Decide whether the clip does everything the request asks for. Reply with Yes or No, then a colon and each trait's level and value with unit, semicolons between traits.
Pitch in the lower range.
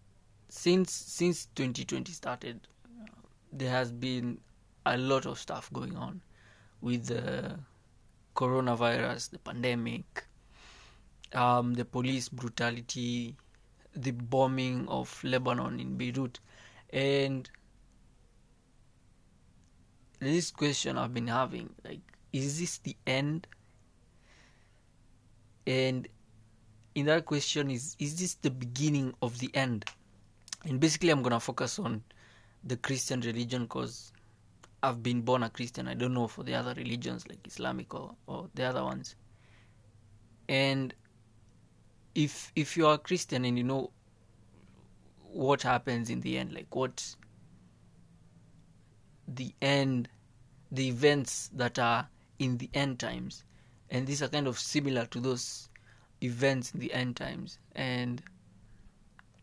Yes: low, 120 Hz